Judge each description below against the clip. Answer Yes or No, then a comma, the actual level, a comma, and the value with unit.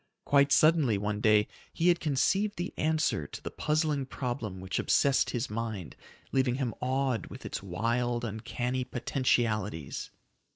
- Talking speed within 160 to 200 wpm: No, average, 140 wpm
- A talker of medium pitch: No, low, 125 Hz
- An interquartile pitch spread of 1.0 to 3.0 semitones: No, average, 4.6 semitones